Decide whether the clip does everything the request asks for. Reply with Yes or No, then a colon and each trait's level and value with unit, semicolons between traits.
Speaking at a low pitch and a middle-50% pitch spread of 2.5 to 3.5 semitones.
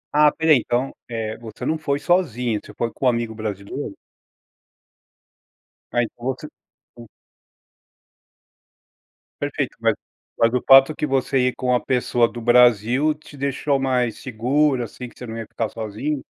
Yes: low, 125 Hz; average, 3.2 semitones